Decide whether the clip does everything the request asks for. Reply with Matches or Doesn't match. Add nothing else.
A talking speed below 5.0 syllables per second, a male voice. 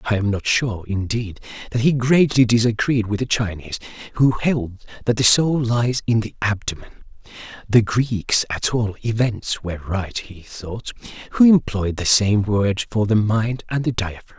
Matches